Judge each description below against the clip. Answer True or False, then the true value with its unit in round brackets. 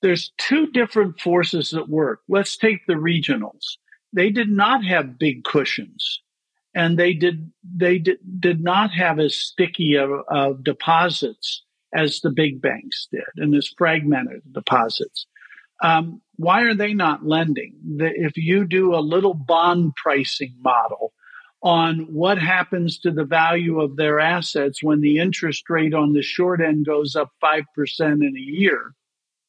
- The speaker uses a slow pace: False (155 wpm)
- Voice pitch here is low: False (165 Hz)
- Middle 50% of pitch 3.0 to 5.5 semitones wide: True (3.3 semitones)